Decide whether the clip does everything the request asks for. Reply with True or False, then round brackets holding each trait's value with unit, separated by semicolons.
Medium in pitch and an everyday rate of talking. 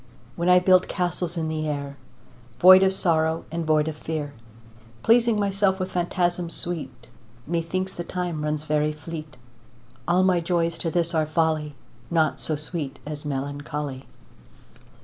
True (165 Hz; 150 wpm)